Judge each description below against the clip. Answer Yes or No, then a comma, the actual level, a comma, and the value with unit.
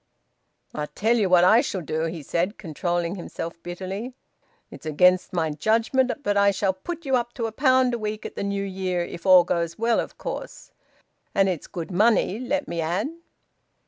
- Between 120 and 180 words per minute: No, average, 190 wpm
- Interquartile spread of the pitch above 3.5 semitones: Yes, average, 4.7 semitones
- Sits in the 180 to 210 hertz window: Yes, high, 190 Hz